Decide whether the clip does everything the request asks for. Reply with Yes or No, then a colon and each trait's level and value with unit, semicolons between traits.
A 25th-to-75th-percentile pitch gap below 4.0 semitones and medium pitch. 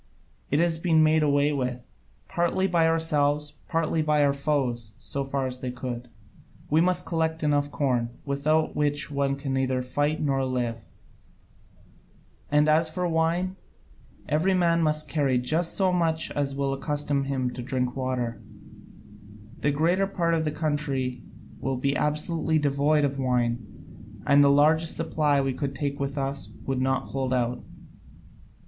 Yes: average, 3.0 semitones; medium, 145 Hz